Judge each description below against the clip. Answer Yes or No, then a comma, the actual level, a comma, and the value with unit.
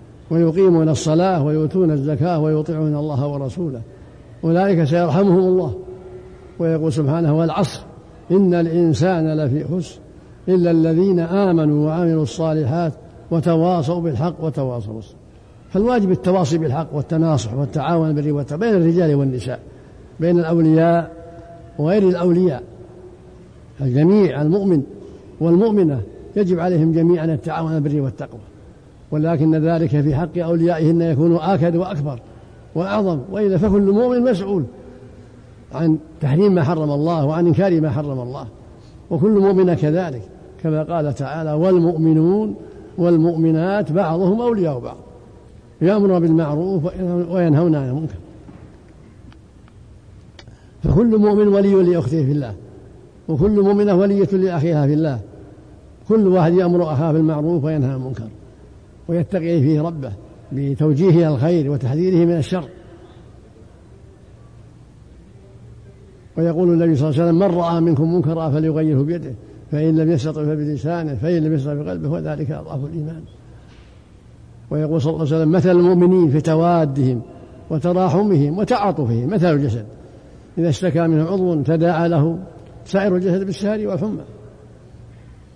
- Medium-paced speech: Yes, average, 110 wpm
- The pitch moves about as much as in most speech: Yes, average, 3.7 semitones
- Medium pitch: Yes, medium, 160 Hz